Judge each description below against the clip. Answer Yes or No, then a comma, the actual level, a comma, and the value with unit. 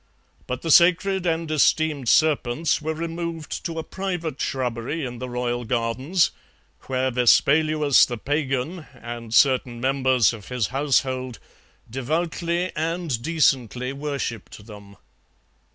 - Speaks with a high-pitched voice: No, low, 135 Hz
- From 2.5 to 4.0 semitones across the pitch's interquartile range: No, average, 4.8 semitones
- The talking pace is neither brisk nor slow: No, slow, 120 wpm